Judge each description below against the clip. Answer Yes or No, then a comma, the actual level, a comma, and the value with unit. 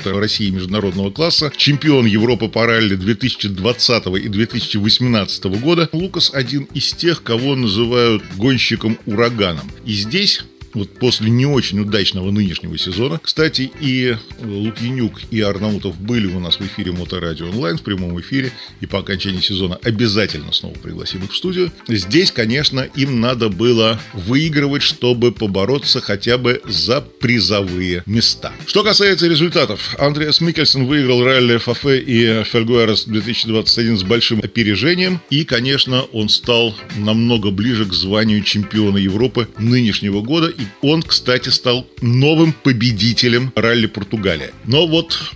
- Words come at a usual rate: Yes, average, 130 wpm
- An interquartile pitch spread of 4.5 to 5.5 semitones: No, average, 4.1 semitones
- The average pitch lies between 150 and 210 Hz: No, low, 115 Hz